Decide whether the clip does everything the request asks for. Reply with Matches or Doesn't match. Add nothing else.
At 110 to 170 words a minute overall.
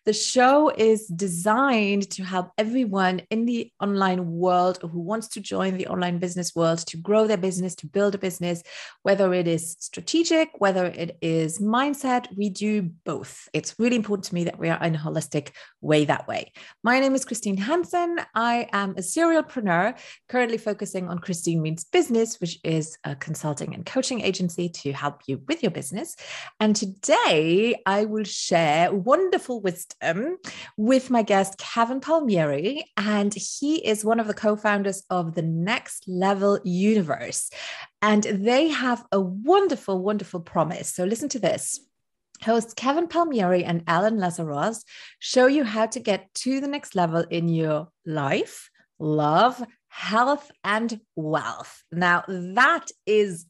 Matches